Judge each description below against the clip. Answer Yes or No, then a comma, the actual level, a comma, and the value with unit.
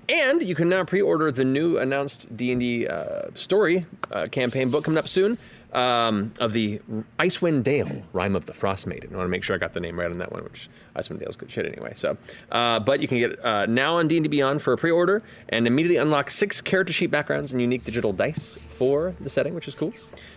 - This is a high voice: No, low, 135 Hz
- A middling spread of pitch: No, wide, 6.3 semitones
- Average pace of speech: No, fast, 240 wpm